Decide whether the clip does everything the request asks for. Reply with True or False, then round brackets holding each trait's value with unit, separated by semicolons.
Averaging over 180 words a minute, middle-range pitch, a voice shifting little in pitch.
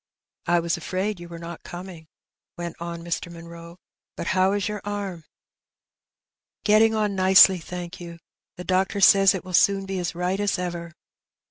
True (190 wpm; 180 Hz; 2.3 semitones)